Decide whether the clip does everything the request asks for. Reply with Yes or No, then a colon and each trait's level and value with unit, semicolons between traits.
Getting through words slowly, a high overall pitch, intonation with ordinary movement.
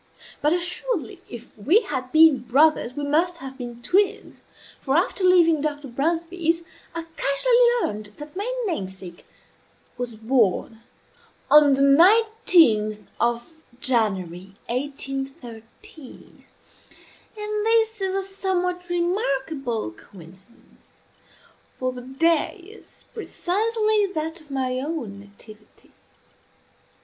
No: slow, 105 wpm; very high, 295 Hz; wide, 7.0 semitones